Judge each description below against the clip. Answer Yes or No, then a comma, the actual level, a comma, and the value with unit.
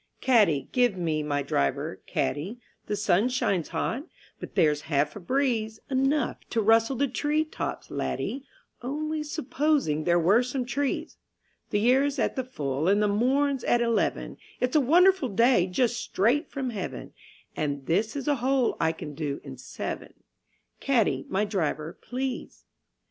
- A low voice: No, high, 230 Hz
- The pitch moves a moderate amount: No, wide, 7.6 semitones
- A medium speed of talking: Yes, average, 155 wpm